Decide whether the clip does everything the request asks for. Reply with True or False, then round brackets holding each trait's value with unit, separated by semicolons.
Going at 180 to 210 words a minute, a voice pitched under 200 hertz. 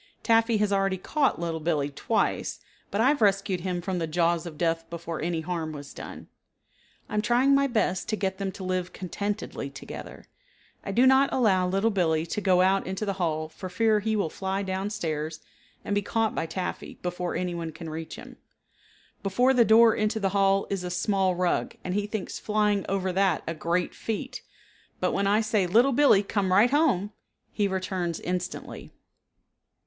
True (190 wpm; 190 Hz)